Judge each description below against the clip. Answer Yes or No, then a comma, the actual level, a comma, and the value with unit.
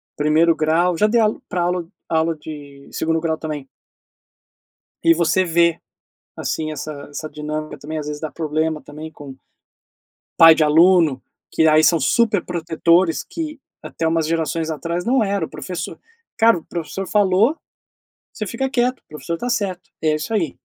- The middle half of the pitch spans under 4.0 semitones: Yes, average, 3.1 semitones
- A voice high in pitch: No, medium, 165 Hz